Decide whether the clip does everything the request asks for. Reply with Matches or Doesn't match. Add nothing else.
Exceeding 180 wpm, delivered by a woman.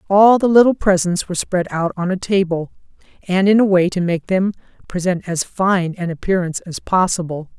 Matches